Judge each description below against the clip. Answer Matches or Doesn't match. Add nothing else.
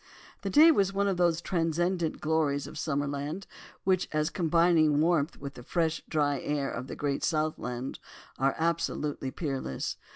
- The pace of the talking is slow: Doesn't match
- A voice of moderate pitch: Matches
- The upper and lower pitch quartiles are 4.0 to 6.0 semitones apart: Doesn't match